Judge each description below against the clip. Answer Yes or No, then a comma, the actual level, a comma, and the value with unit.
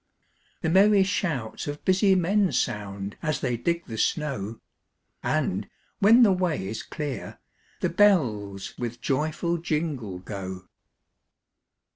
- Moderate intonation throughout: No, wide, 8.8 semitones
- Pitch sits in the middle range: Yes, medium, 150 Hz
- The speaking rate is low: Yes, slow, 120 wpm